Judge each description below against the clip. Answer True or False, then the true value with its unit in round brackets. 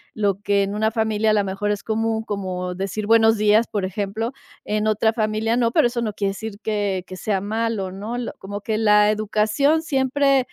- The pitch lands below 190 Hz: False (215 Hz)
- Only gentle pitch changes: True (1.8 semitones)